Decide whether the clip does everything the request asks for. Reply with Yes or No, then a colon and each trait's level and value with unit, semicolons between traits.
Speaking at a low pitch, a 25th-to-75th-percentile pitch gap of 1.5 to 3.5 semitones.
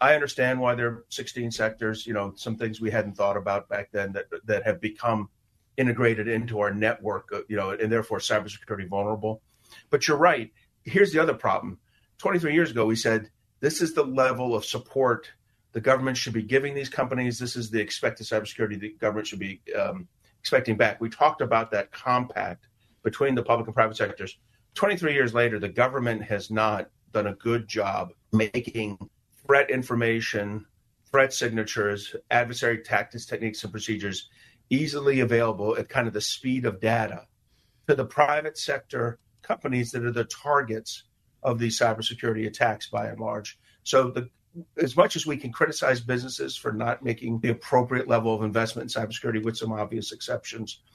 Yes: low, 115 Hz; narrow, 2.6 semitones